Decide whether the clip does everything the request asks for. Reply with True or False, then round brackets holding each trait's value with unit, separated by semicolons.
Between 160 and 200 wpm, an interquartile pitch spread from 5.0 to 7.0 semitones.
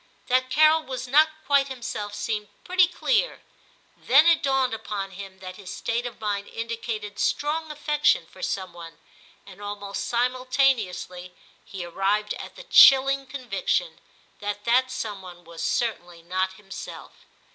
False (145 wpm; 5.6 semitones)